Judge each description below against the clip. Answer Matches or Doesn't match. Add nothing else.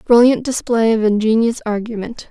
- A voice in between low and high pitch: Doesn't match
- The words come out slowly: Matches